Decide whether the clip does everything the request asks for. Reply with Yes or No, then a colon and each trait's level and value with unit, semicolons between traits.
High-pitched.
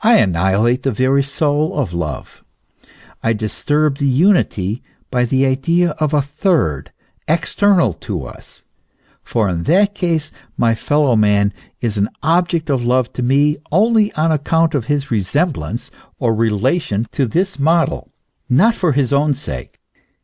No: medium, 140 Hz